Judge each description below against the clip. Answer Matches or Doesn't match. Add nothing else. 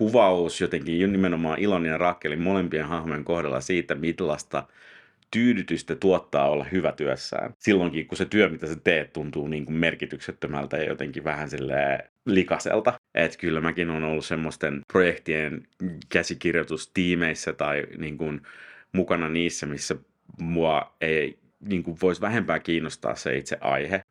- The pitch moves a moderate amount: Doesn't match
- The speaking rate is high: Doesn't match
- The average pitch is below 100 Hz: Matches